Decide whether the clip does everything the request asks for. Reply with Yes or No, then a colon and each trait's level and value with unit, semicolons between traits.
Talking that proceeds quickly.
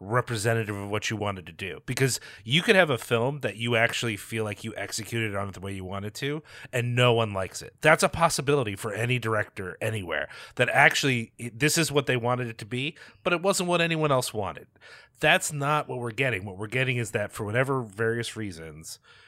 Yes: fast, 220 wpm